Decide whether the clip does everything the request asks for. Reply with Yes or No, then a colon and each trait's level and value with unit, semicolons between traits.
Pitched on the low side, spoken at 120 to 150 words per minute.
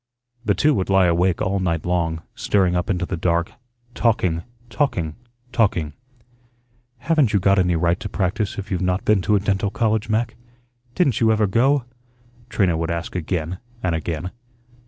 No: very low, 95 Hz; average, 170 wpm